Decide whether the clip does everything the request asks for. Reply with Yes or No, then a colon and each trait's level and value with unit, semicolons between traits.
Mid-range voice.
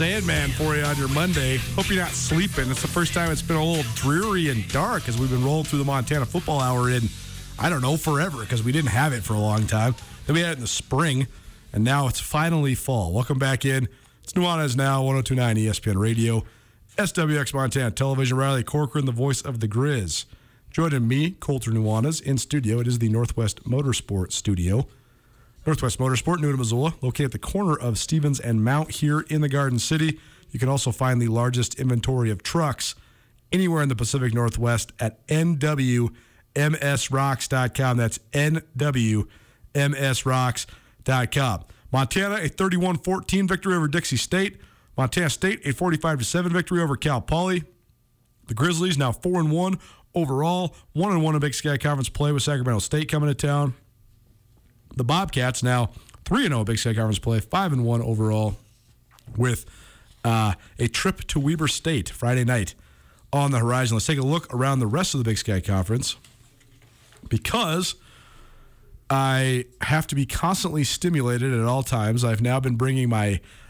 No: low, 130 Hz